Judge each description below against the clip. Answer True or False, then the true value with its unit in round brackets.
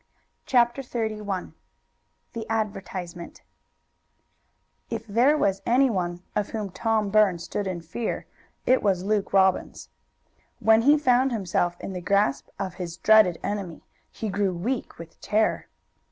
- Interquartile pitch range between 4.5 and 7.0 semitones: False (3.6 semitones)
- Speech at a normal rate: False (130 wpm)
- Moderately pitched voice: False (205 Hz)